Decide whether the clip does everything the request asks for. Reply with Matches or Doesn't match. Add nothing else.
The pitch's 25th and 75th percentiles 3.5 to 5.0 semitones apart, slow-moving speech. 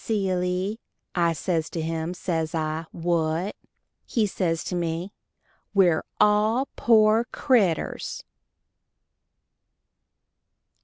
Matches